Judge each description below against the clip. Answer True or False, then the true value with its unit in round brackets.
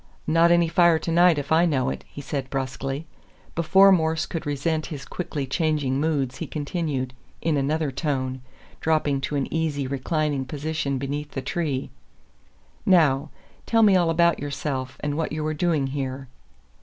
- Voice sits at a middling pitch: True (150 Hz)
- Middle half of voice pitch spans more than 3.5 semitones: False (3.1 semitones)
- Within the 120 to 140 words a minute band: False (160 wpm)